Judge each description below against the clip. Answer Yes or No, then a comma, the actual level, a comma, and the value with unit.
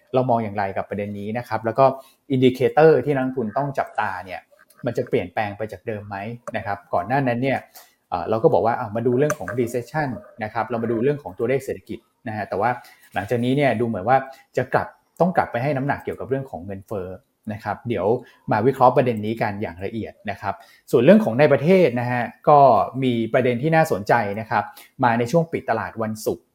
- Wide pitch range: No, average, 3.5 semitones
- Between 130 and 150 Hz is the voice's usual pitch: No, low, 120 Hz